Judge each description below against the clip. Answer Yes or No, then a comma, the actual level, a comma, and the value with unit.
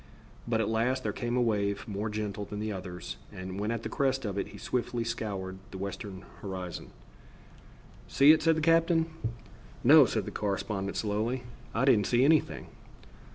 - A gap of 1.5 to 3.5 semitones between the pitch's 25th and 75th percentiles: No, average, 4.0 semitones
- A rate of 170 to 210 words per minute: Yes, average, 175 wpm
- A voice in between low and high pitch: No, low, 110 Hz